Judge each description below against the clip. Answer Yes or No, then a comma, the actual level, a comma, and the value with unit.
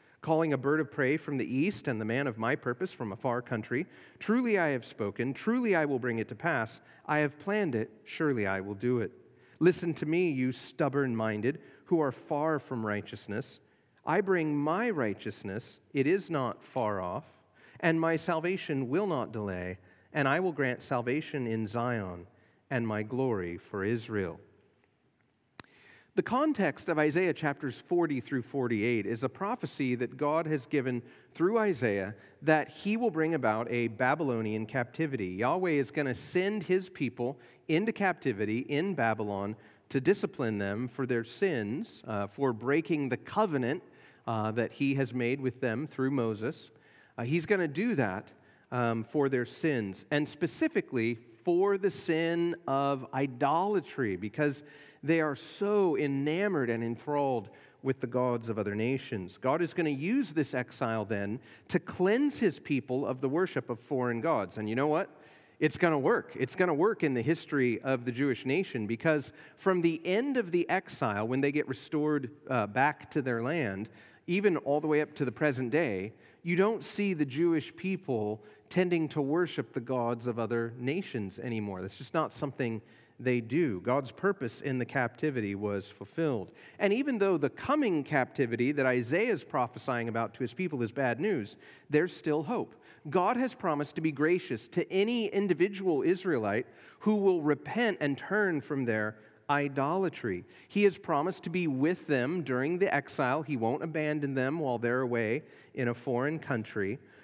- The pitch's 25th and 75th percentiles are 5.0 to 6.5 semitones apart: Yes, wide, 5.6 semitones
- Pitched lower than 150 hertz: Yes, medium, 140 Hz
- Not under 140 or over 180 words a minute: Yes, average, 175 wpm